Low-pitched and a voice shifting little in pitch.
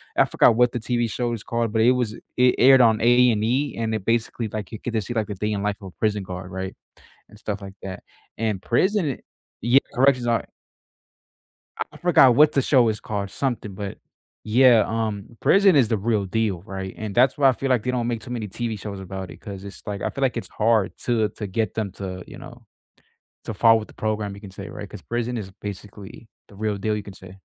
No: low, 110 Hz; average, 3.2 semitones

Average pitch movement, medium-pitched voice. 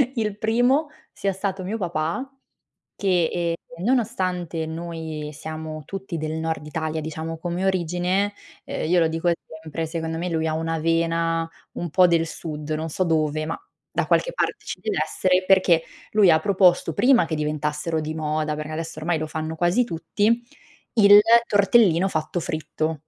Yes: average, 3.0 semitones; medium, 165 Hz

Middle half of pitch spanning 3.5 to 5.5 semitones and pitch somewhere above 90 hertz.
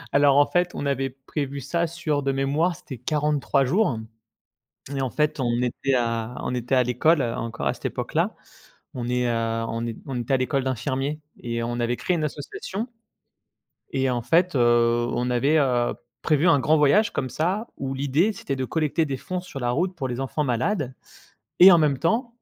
Yes: average, 4.0 semitones; low, 135 Hz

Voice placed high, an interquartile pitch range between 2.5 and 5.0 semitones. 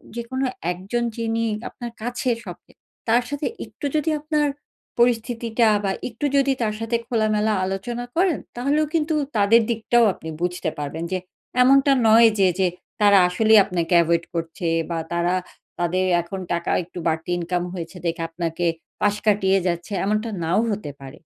No: high, 210 Hz; wide, 5.4 semitones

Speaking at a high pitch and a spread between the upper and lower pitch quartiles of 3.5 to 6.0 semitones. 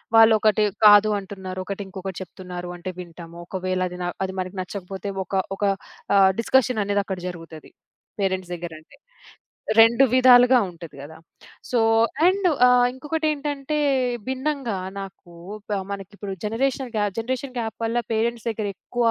Yes: high, 205 Hz; average, 5.0 semitones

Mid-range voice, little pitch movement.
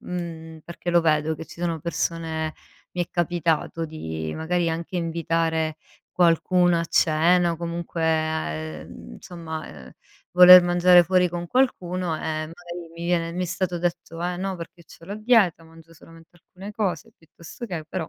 Yes: medium, 170 Hz; narrow, 1.6 semitones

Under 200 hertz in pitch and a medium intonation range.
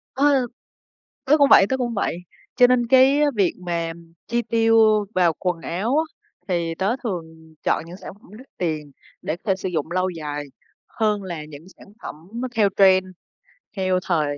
No: medium, 185 Hz; wide, 5.9 semitones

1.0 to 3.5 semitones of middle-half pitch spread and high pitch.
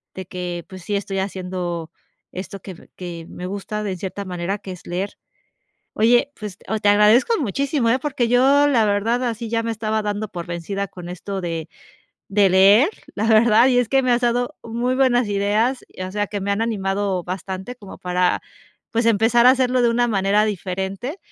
No: average, 4.0 semitones; high, 205 Hz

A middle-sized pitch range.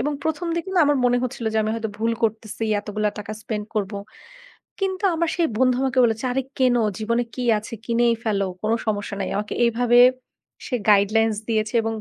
Yes: average, 3.0 semitones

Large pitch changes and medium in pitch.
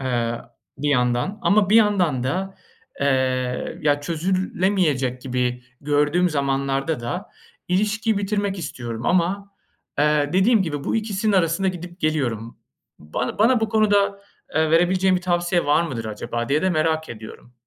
Yes: wide, 6.5 semitones; medium, 160 Hz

